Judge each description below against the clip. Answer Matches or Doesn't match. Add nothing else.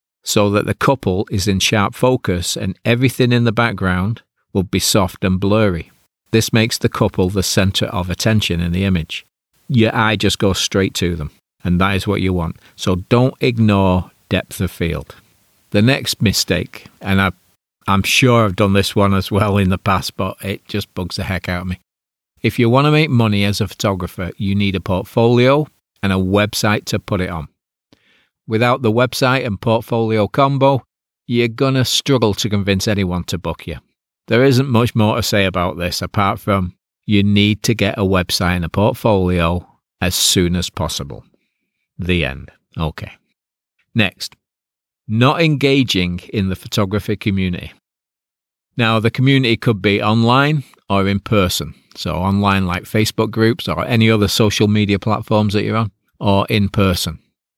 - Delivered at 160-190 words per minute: Matches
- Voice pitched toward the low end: Matches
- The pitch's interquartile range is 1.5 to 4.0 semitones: Matches